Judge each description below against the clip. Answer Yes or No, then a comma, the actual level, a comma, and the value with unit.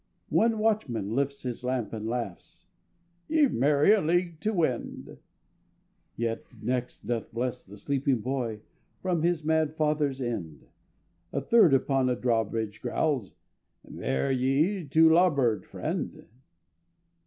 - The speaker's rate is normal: No, slow, 125 wpm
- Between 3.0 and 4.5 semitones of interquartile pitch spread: No, average, 5.3 semitones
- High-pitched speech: No, low, 135 Hz